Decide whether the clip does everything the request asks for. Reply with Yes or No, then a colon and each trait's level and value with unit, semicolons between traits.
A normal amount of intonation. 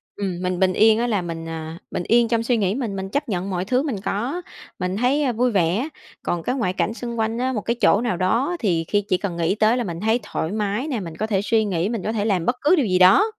Yes: average, 4.5 semitones